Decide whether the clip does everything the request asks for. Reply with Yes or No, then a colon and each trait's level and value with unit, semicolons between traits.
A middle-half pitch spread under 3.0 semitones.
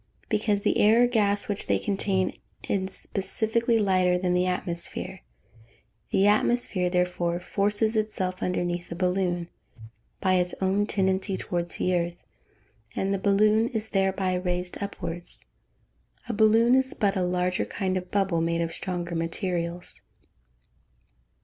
Yes: narrow, 2.4 semitones